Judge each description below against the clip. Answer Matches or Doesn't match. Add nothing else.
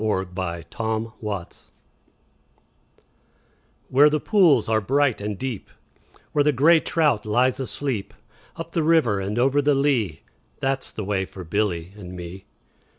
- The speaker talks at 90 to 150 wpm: Matches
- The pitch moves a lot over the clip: Matches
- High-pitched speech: Doesn't match